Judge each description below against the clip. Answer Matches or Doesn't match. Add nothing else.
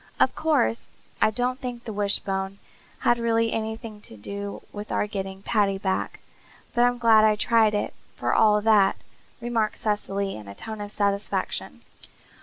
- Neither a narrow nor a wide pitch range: Doesn't match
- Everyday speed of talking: Matches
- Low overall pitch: Doesn't match